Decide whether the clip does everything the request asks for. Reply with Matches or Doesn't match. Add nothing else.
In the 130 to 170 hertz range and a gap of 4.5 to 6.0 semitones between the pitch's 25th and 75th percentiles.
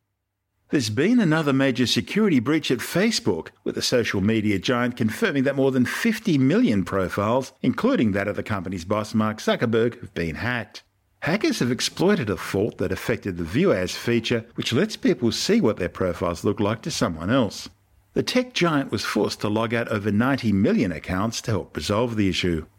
Doesn't match